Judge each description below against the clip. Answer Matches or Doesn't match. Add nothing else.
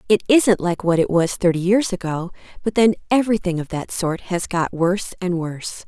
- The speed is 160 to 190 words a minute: Doesn't match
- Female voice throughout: Matches